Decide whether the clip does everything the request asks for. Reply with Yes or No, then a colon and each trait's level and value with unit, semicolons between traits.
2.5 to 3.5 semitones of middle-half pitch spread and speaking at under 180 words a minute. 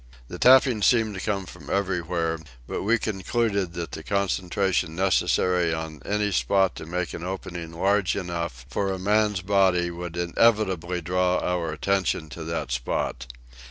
Yes: average, 2.8 semitones; average, 155 wpm